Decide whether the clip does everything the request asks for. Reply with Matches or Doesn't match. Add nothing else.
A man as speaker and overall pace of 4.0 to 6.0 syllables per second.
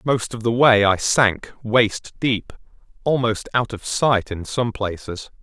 Doesn't match